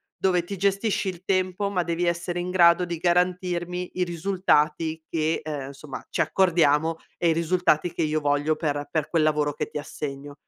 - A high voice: No, medium, 170 Hz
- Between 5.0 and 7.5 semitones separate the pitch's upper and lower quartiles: No, average, 2.8 semitones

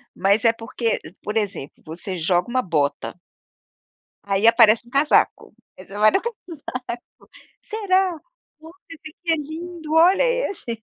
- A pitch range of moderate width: No, wide, 8.3 semitones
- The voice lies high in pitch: Yes, high, 235 Hz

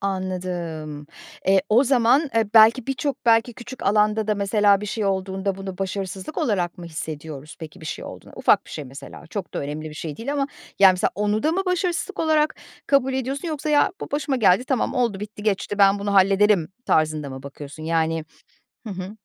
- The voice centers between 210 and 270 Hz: No, high, 200 Hz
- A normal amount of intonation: No, wide, 5.8 semitones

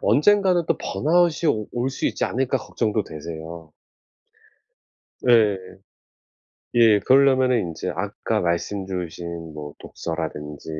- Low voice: Yes, low, 105 Hz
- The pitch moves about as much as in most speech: No, wide, 7.8 semitones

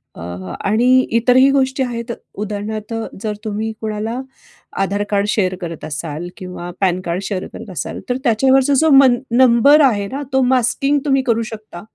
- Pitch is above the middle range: Yes, high, 220 Hz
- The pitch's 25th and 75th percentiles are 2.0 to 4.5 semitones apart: No, average, 4.9 semitones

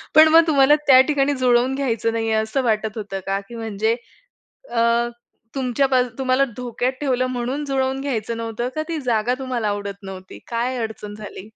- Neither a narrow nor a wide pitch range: Yes, average, 3.4 semitones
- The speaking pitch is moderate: No, high, 245 Hz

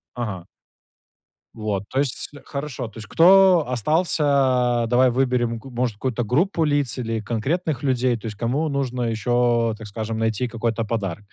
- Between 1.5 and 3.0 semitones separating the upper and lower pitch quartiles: No, average, 3.6 semitones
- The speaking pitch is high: No, low, 120 Hz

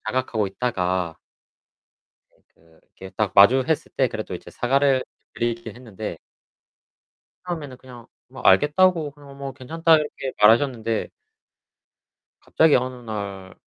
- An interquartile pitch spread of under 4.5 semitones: No, average, 5.2 semitones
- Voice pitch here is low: Yes, low, 125 Hz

